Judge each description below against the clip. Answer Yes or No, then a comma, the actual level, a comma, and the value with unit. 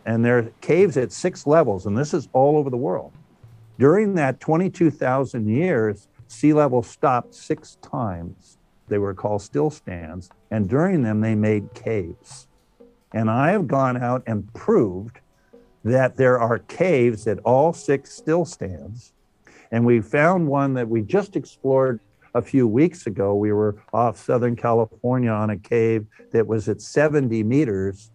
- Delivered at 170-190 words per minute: No, average, 155 wpm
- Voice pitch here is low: Yes, low, 120 Hz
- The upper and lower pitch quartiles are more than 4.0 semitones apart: Yes, average, 4.5 semitones